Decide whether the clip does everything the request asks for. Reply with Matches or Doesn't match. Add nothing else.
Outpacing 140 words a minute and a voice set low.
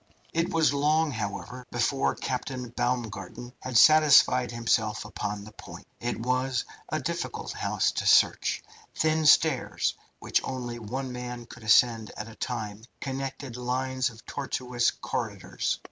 Doesn't match